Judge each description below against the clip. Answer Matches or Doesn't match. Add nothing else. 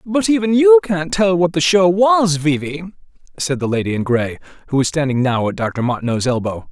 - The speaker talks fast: Matches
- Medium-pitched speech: Matches